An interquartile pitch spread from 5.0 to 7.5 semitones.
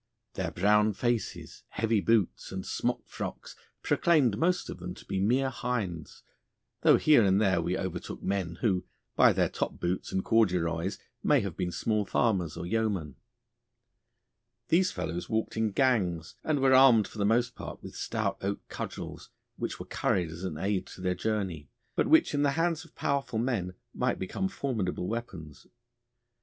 Yes: average, 5.3 semitones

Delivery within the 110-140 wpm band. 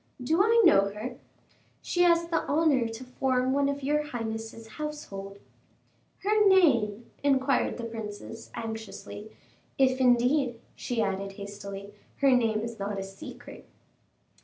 Yes: slow, 135 wpm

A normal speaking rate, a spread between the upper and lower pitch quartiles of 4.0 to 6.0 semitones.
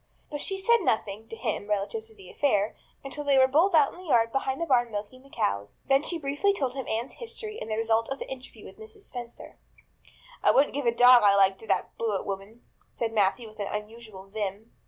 No: fast, 225 wpm; average, 4.9 semitones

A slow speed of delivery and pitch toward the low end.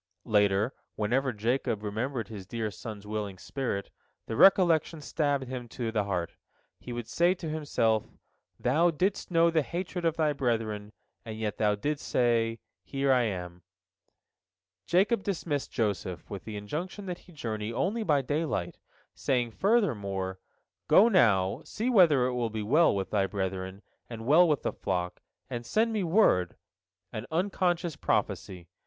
No: average, 150 wpm; low, 120 Hz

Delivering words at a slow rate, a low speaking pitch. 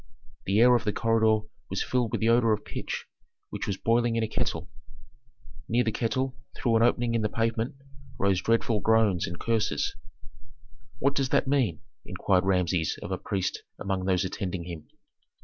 No: average, 175 wpm; low, 110 Hz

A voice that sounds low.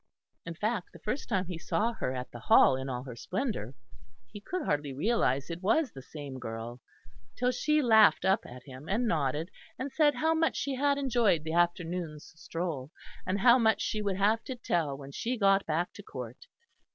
No: medium, 180 Hz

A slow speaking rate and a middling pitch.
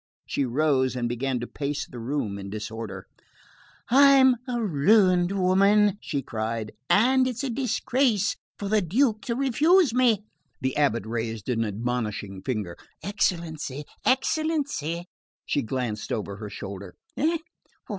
Yes: slow, 130 wpm; medium, 150 Hz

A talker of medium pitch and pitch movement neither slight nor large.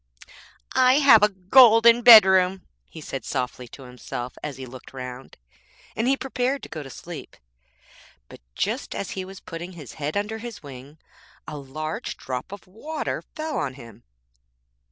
No: medium, 180 Hz; wide, 8.9 semitones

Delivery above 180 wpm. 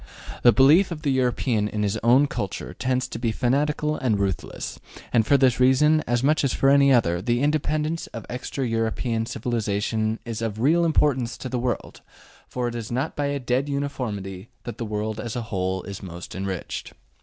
Yes: average, 190 wpm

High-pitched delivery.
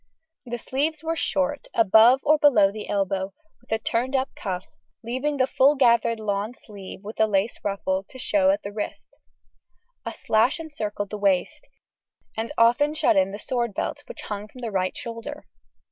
Yes: high, 230 Hz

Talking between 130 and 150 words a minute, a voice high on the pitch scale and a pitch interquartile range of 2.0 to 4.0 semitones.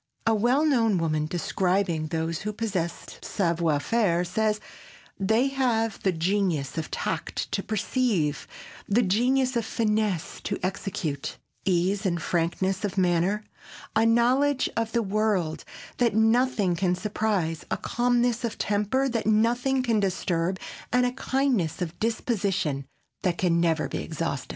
No: average, 140 wpm; high, 205 Hz; average, 5.1 semitones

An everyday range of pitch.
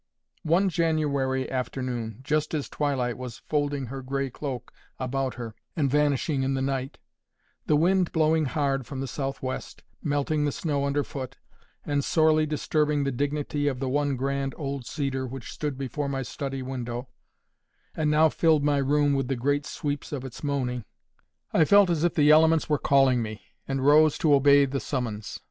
No: narrow, 2.1 semitones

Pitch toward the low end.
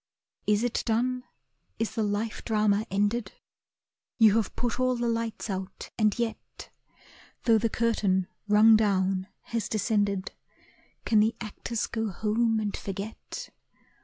No: high, 220 Hz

